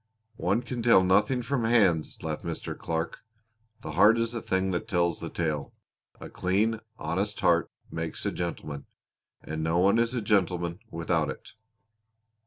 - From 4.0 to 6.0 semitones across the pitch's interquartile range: Yes, average, 5.0 semitones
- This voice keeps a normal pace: Yes, average, 160 wpm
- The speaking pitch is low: Yes, very low, 95 Hz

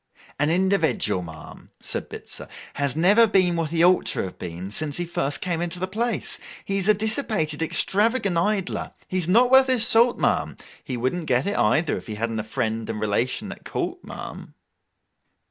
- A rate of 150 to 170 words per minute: No, average, 190 wpm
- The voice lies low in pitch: No, medium, 175 Hz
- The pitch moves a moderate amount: No, wide, 7.8 semitones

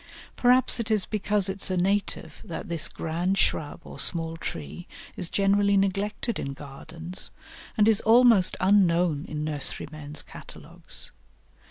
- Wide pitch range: No, average, 4.0 semitones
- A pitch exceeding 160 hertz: Yes, medium, 185 Hz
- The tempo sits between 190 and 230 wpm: No, average, 140 wpm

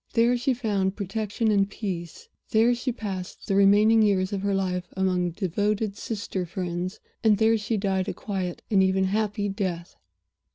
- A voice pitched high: Yes, high, 200 Hz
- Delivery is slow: No, average, 170 wpm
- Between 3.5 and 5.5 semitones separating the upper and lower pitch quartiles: No, narrow, 2.4 semitones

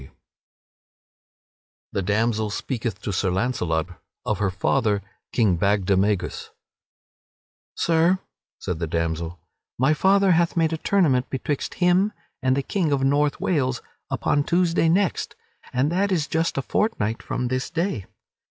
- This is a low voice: Yes, low, 130 Hz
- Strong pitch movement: Yes, wide, 8.6 semitones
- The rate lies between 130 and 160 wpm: Yes, slow, 135 wpm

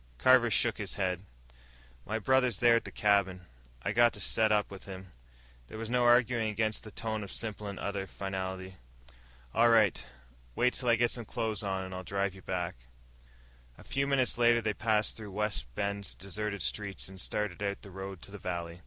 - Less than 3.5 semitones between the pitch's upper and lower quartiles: Yes, average, 3.0 semitones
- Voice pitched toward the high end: No, low, 105 Hz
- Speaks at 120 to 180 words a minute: No, average, 195 wpm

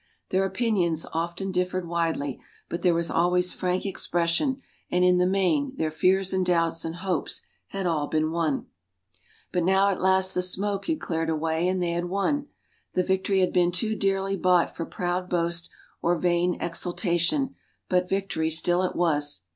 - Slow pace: No, average, 170 wpm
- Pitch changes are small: Yes, narrow, 2.1 semitones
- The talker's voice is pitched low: No, medium, 180 Hz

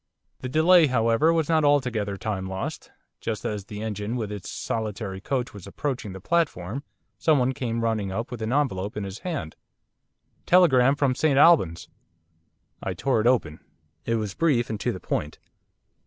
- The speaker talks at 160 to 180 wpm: Yes, average, 170 wpm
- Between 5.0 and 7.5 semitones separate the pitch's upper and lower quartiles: Yes, wide, 5.5 semitones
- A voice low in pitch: Yes, low, 115 Hz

